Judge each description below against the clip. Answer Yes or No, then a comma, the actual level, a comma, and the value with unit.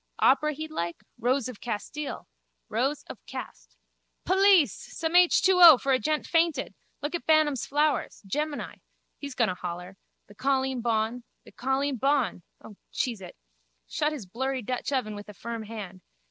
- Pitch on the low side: No, very high, 265 Hz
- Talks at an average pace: Yes, average, 160 wpm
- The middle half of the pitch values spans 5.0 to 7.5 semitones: Yes, wide, 5.6 semitones